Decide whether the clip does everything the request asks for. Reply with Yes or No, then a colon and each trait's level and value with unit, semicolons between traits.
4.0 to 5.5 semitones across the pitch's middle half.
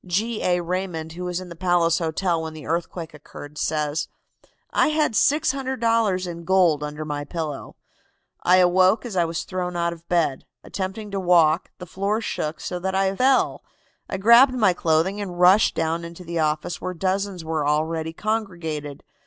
No: average, 3.1 semitones